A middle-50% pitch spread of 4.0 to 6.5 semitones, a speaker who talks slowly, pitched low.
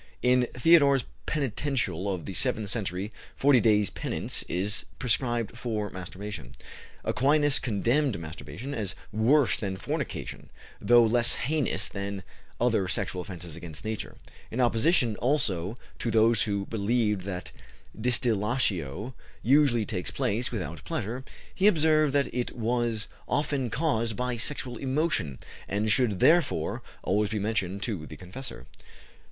Yes: average, 4.4 semitones; slow, 130 wpm; low, 115 Hz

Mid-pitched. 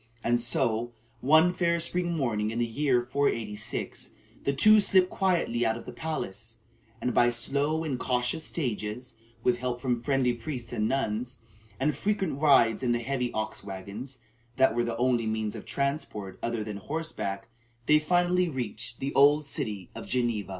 No: low, 125 Hz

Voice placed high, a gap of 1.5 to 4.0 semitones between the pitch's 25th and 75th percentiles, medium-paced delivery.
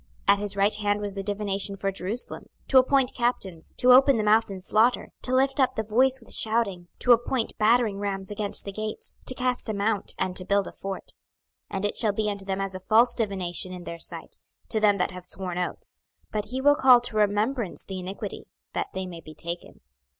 No: high, 205 Hz; average, 3.5 semitones; fast, 225 wpm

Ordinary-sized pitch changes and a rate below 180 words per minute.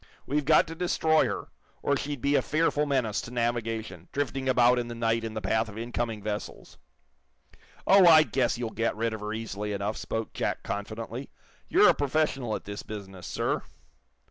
No: average, 4.3 semitones; average, 185 wpm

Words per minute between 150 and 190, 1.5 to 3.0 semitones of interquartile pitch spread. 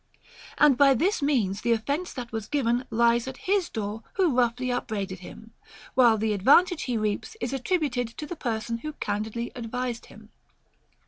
No: average, 175 wpm; average, 4.3 semitones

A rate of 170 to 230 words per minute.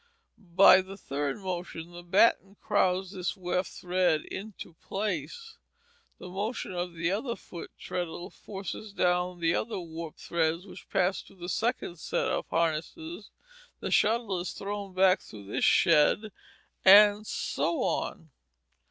No: average, 145 wpm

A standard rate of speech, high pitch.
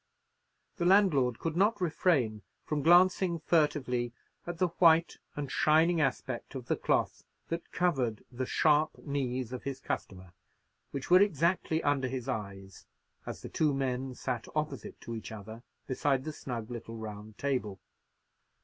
No: average, 150 wpm; low, 135 Hz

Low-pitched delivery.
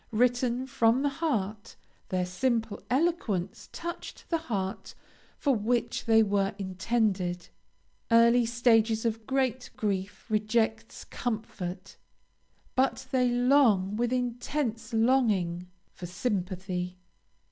No: high, 225 Hz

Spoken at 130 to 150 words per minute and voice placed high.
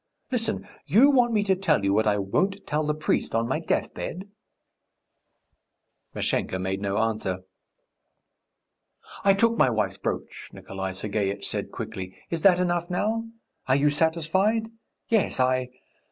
No: average, 140 wpm; medium, 150 Hz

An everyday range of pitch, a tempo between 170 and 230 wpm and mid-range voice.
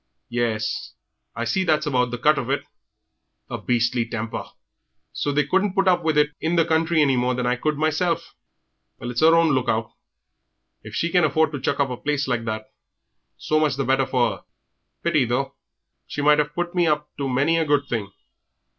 Yes: average, 4.3 semitones; fast, 205 wpm; medium, 145 Hz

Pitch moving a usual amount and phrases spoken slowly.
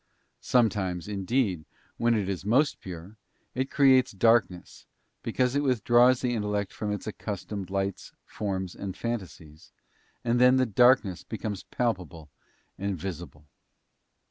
Yes: average, 4.5 semitones; slow, 130 wpm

